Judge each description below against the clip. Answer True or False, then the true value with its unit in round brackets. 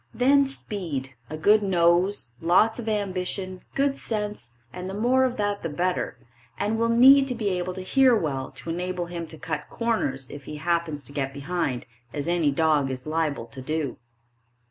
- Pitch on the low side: False (175 Hz)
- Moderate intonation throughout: False (5.8 semitones)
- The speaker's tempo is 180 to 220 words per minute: True (185 wpm)